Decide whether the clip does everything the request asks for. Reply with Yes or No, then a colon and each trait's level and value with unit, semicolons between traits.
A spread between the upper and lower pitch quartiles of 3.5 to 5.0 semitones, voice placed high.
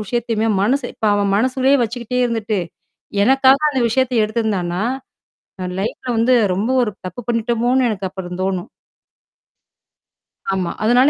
Yes: average, 3.8 semitones; high, 230 Hz